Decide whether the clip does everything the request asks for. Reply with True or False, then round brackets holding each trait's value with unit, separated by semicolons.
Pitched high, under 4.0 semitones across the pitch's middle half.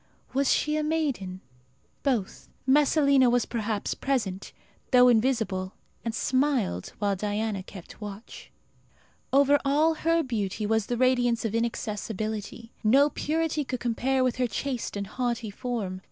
False (240 Hz; 4.5 semitones)